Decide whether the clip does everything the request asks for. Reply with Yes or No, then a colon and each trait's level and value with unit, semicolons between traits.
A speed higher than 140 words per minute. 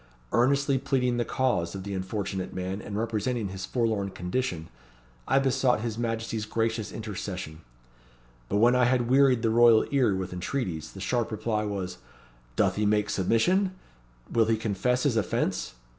Yes: average, 160 wpm